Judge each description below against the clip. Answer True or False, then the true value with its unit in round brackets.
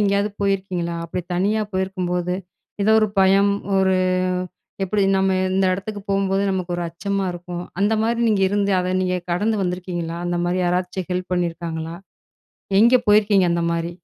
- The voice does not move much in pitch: True (2.1 semitones)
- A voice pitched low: False (185 Hz)